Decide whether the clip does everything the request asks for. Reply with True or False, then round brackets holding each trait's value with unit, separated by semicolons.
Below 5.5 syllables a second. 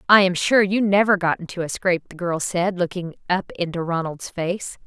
True (5.2 syllables/s)